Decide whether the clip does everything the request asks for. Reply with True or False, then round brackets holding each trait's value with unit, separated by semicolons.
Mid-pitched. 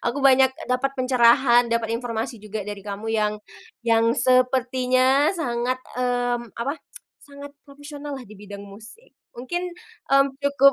False (250 Hz)